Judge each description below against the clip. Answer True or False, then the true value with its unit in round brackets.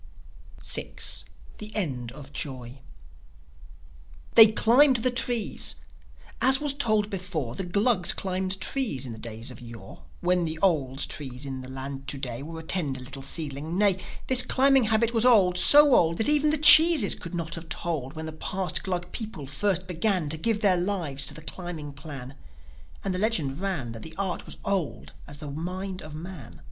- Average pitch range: False (6.9 semitones)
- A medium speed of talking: True (180 wpm)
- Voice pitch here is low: False (175 Hz)